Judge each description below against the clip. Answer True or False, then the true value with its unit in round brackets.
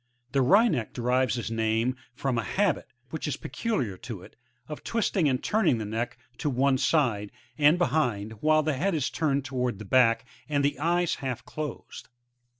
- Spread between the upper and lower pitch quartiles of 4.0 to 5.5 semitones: True (4.9 semitones)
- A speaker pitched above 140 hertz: False (135 Hz)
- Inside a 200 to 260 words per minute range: False (175 wpm)